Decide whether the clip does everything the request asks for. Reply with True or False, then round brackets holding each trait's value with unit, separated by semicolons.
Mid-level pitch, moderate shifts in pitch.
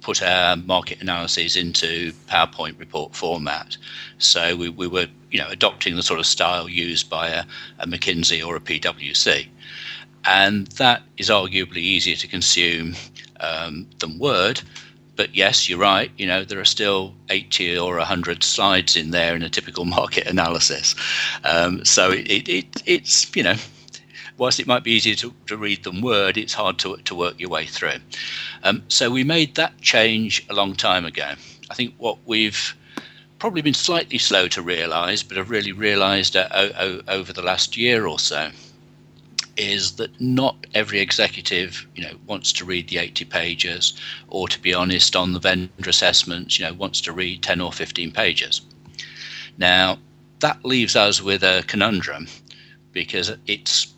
False (95 Hz; 3.4 semitones)